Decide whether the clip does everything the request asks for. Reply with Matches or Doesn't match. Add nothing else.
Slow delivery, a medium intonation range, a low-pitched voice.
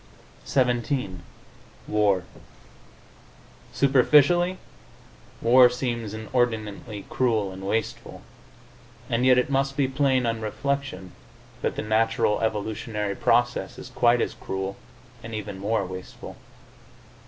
Matches